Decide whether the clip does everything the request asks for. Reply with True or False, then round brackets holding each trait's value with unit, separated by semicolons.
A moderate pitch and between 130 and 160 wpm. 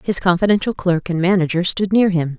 False (180 Hz; 200 wpm)